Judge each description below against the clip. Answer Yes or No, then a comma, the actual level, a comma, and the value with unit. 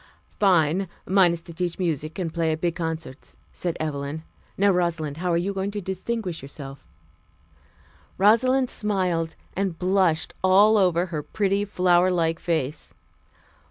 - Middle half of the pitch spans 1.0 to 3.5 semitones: Yes, average, 3.0 semitones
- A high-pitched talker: No, medium, 175 Hz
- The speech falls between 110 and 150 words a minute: Yes, average, 145 wpm